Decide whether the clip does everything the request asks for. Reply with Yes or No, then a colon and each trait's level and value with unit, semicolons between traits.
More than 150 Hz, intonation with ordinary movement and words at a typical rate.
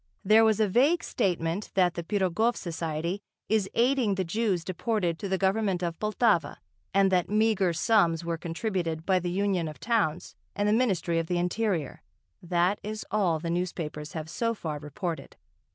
Yes: medium, 185 Hz; average, 4.1 semitones; average, 170 wpm